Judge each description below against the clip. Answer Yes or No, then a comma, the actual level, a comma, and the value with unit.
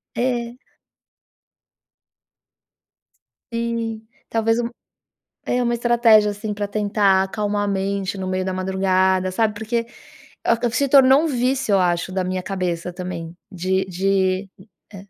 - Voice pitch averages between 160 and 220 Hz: Yes, high, 200 Hz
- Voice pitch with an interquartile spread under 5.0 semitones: Yes, average, 3.7 semitones